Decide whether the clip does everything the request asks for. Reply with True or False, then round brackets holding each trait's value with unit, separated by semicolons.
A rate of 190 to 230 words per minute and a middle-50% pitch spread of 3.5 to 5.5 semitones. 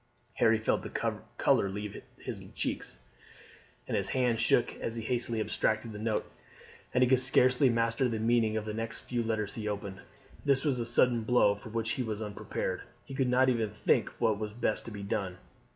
False (200 wpm; 2.5 semitones)